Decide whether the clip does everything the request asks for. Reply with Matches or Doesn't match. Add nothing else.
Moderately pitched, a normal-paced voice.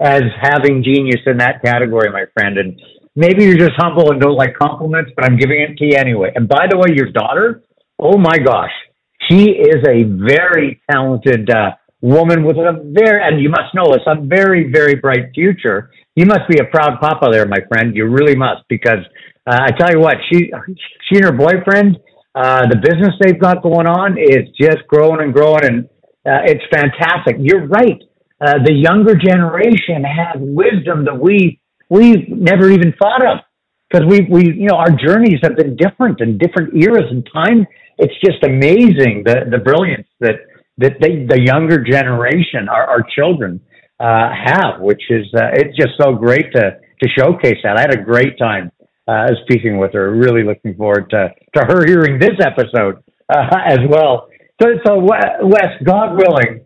Matches